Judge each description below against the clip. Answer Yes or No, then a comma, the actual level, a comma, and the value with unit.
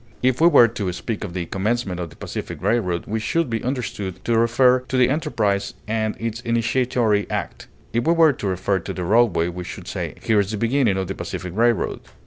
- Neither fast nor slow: No, fast, 215 wpm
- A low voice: Yes, low, 115 Hz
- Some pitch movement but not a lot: Yes, average, 4.0 semitones